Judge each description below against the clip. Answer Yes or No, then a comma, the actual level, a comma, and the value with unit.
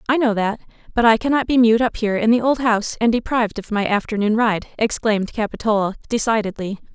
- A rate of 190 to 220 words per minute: Yes, average, 200 wpm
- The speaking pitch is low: No, high, 220 Hz